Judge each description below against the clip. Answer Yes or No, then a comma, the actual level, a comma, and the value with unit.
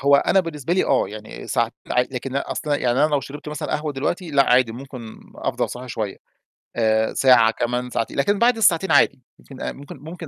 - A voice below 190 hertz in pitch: Yes, low, 135 Hz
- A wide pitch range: No, average, 3.6 semitones